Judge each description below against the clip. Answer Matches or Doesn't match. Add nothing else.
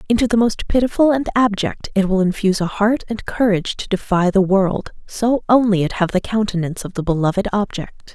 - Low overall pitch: Doesn't match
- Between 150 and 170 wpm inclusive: Doesn't match